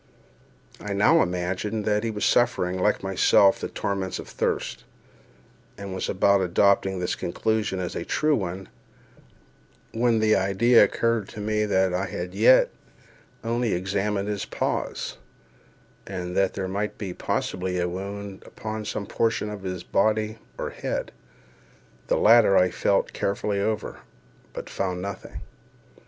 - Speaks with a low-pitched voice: Yes, low, 100 Hz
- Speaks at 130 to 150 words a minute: Yes, average, 145 wpm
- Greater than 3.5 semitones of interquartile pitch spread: No, narrow, 2.4 semitones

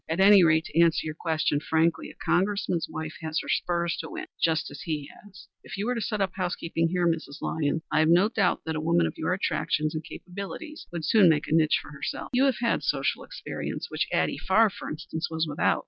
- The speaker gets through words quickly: Yes, fast, 230 wpm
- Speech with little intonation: No, average, 3.3 semitones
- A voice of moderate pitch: Yes, medium, 165 Hz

